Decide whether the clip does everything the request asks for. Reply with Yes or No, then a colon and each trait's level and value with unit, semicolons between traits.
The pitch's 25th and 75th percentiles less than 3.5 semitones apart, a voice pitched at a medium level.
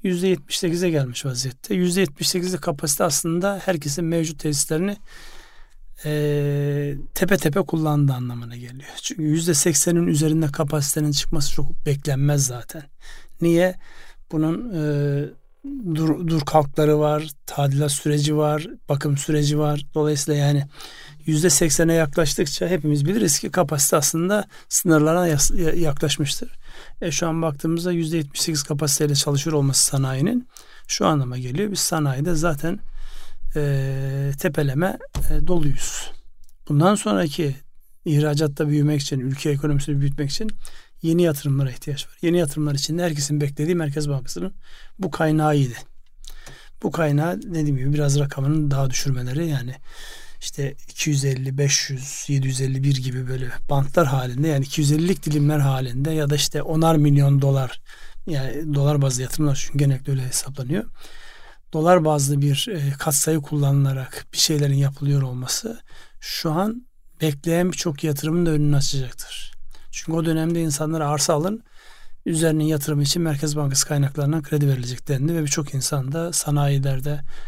Yes: average, 2.8 semitones; medium, 150 Hz